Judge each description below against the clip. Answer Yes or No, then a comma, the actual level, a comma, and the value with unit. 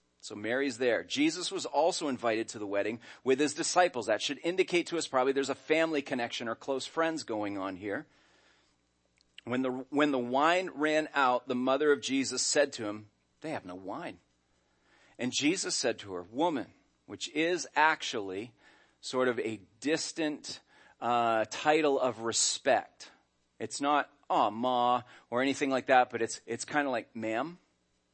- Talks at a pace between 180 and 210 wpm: No, average, 170 wpm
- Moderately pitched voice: No, low, 125 Hz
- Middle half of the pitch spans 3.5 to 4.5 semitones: No, average, 5.3 semitones